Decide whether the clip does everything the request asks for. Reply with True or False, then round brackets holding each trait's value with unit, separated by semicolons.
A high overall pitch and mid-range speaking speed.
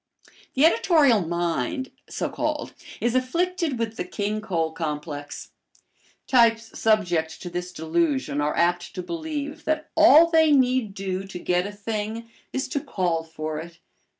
True (215 Hz; 150 wpm)